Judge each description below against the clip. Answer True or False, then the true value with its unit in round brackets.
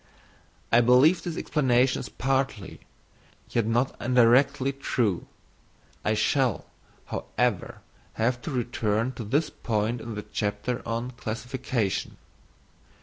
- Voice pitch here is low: True (120 Hz)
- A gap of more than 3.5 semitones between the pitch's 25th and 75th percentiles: False (2.8 semitones)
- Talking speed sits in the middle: False (110 wpm)